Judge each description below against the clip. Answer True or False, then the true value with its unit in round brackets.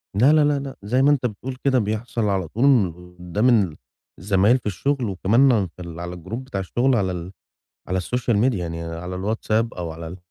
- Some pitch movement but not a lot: False (5.8 semitones)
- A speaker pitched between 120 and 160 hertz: False (105 Hz)